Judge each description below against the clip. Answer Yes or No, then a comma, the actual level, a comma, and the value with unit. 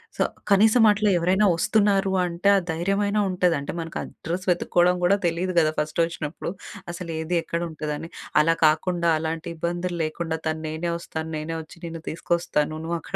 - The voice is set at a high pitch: No, medium, 170 Hz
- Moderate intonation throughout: No, narrow, 2.2 semitones